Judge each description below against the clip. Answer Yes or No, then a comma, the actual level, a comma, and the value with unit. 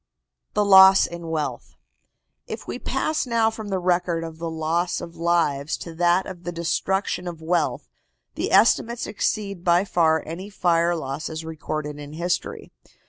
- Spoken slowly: No, average, 155 wpm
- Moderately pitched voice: Yes, medium, 170 Hz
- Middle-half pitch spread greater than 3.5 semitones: No, average, 2.8 semitones